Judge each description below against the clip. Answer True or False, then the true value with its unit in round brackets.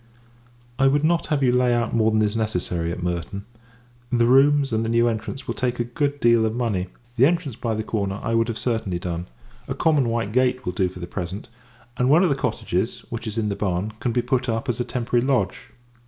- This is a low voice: True (115 Hz)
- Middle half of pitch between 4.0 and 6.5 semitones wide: False (3.5 semitones)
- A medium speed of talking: False (235 wpm)